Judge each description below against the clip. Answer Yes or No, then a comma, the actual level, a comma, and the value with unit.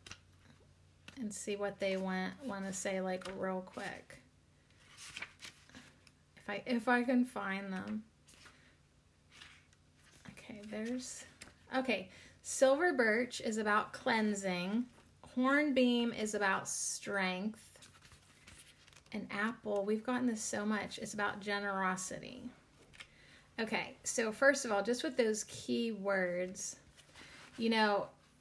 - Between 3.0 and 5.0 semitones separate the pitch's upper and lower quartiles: Yes, average, 4.0 semitones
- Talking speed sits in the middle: No, slow, 110 wpm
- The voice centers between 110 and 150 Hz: No, high, 210 Hz